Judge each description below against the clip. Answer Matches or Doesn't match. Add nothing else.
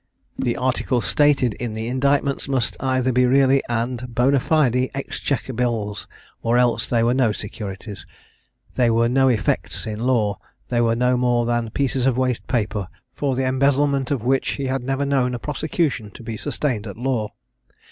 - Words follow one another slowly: Doesn't match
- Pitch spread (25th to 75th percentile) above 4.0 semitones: Doesn't match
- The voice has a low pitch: Matches